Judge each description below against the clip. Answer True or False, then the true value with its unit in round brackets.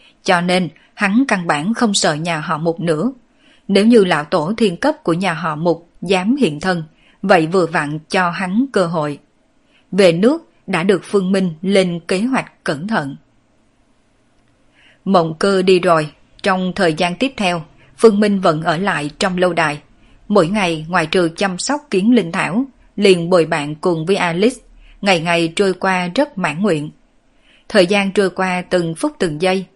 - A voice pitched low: False (185 Hz)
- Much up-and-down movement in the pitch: False (3.6 semitones)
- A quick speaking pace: False (180 wpm)